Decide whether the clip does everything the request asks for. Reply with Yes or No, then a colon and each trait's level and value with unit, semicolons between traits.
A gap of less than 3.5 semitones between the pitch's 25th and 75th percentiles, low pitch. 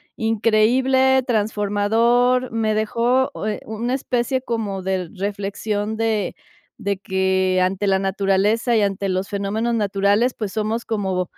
No: average, 2.9 semitones; high, 215 Hz